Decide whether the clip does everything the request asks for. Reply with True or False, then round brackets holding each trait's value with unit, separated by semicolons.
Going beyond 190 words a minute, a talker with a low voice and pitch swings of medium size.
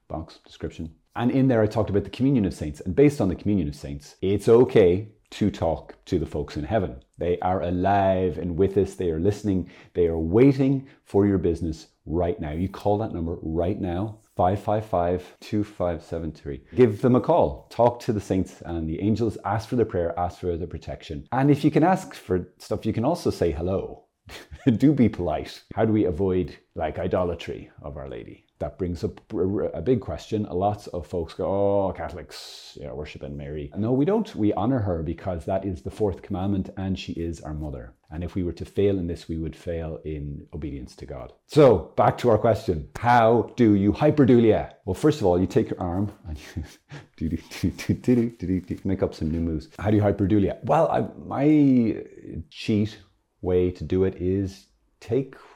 True (200 wpm; 95 Hz; 4.1 semitones)